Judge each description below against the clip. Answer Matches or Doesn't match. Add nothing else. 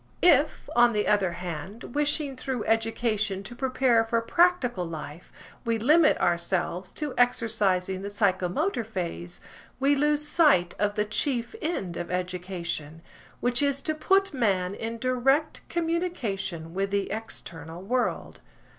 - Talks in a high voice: Matches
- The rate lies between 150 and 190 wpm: Doesn't match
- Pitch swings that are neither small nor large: Doesn't match